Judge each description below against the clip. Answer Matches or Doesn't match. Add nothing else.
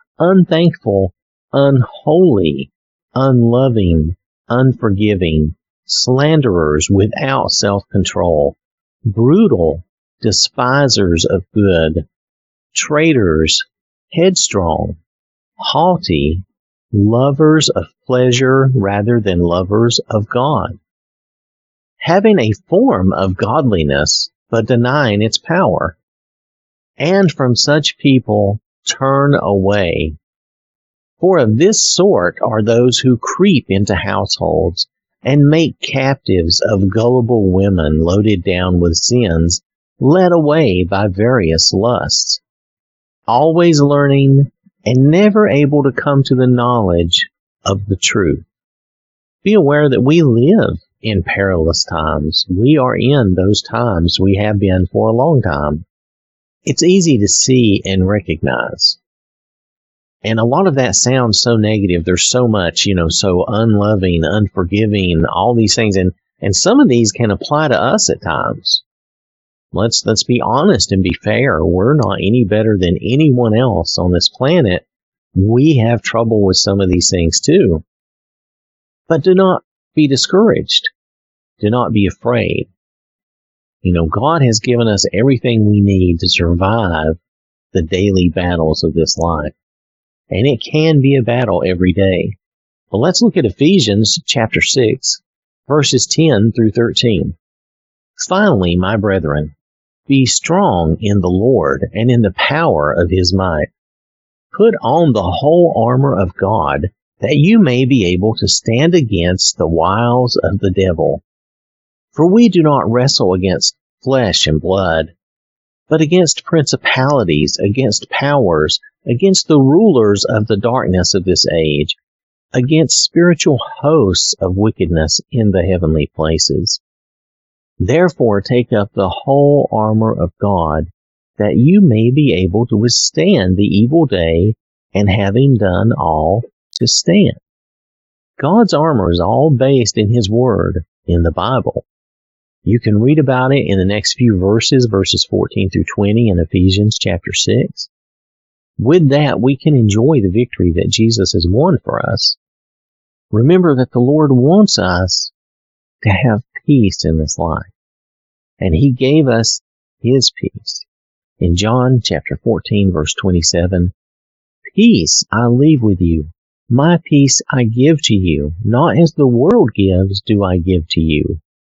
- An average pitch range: Doesn't match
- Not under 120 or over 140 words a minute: Matches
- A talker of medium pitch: Doesn't match